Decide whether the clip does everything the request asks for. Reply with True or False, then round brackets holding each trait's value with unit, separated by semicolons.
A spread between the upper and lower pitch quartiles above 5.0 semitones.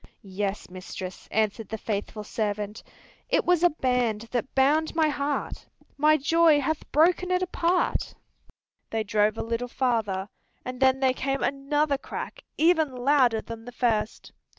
True (5.5 semitones)